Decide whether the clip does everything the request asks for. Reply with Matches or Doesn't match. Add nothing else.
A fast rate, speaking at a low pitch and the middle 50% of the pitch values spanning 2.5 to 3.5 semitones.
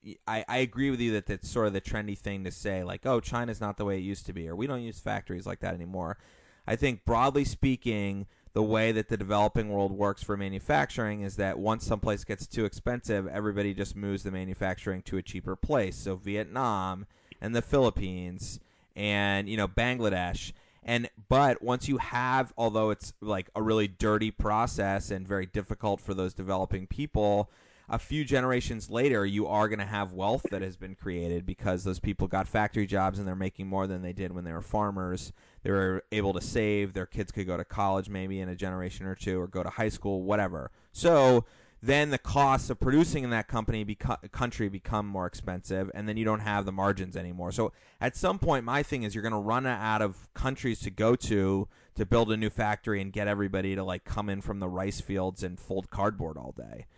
Matches